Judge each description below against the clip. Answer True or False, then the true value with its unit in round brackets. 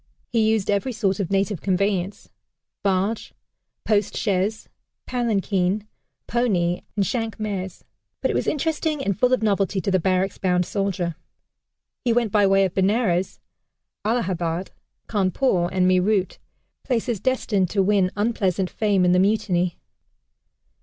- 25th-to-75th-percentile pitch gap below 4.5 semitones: True (2.9 semitones)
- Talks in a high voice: True (200 Hz)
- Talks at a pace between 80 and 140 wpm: True (135 wpm)